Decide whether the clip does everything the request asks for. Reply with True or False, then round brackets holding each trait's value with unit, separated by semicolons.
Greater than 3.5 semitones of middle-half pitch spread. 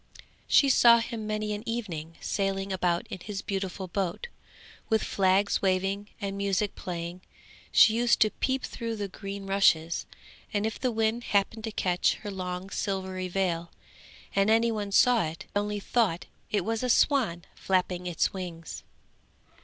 False (3.0 semitones)